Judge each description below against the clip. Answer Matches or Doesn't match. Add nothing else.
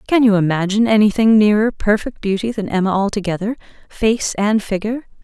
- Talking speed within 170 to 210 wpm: Doesn't match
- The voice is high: Matches